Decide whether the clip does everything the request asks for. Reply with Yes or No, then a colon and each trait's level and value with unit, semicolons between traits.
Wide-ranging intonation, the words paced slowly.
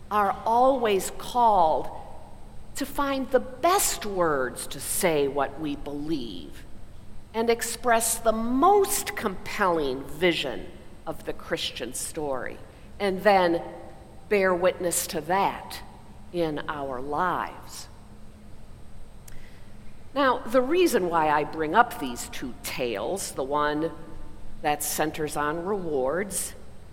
Yes: wide, 7.7 semitones; slow, 105 wpm